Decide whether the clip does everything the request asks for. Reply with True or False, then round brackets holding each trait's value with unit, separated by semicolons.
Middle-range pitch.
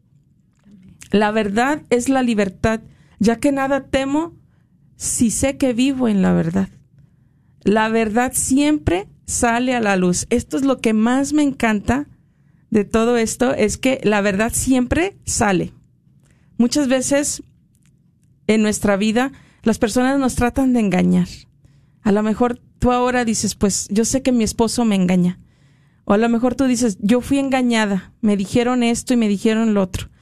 False (230 Hz)